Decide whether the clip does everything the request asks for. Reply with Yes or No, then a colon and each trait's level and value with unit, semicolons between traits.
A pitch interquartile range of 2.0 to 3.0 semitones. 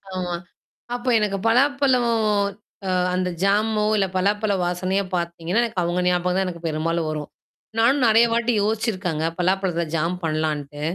No: average, 4.4 semitones